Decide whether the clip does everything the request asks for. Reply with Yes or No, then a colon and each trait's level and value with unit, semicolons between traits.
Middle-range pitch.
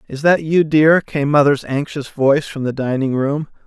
Yes: medium, 145 Hz